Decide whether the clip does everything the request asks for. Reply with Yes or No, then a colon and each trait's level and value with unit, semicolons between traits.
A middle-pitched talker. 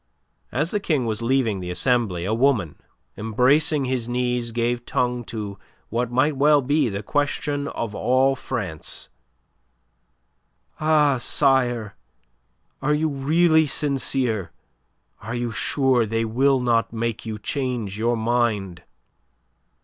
No: low, 120 Hz